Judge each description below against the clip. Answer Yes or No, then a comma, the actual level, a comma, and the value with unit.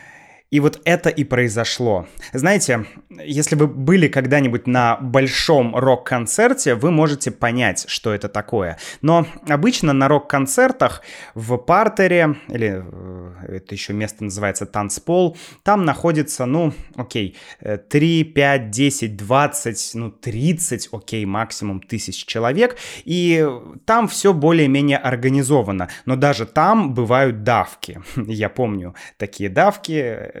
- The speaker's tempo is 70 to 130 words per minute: Yes, average, 115 wpm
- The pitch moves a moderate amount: No, wide, 5.9 semitones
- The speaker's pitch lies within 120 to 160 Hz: Yes, low, 135 Hz